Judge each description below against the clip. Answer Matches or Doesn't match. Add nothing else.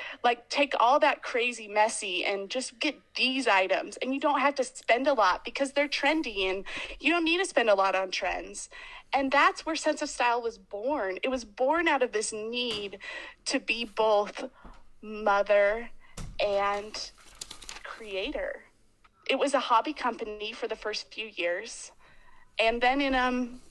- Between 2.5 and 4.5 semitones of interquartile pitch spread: Doesn't match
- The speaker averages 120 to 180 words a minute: Matches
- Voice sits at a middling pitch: Doesn't match